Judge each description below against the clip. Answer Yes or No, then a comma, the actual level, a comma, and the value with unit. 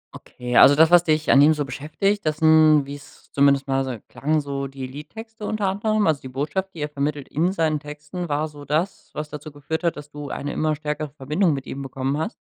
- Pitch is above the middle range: No, medium, 150 Hz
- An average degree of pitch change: No, narrow, 2.2 semitones